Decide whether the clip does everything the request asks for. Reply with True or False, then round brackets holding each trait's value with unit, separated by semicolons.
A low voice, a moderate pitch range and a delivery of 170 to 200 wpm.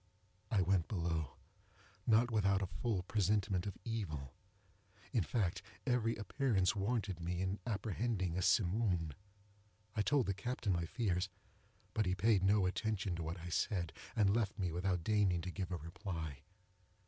False (95 Hz; 3.6 semitones; 150 wpm)